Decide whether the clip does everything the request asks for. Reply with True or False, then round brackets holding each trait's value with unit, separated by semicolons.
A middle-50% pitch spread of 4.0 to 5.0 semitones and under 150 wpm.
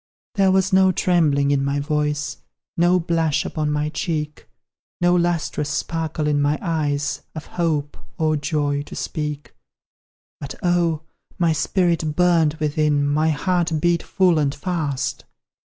False (2.7 semitones; 135 wpm)